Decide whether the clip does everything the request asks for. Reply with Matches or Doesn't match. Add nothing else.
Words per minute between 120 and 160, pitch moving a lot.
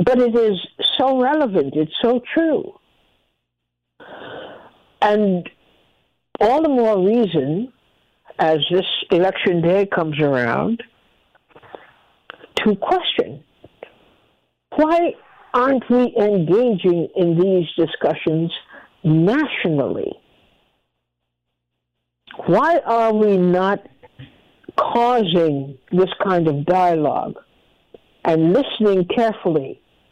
Doesn't match